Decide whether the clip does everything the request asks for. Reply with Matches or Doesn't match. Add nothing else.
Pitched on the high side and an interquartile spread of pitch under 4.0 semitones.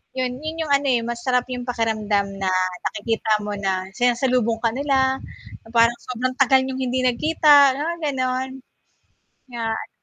Matches